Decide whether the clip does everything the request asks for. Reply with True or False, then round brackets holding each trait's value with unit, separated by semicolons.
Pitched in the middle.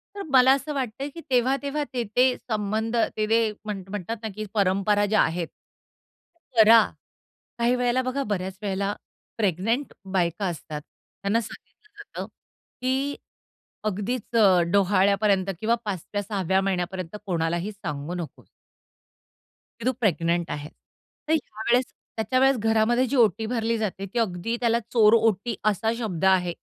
False (215 Hz)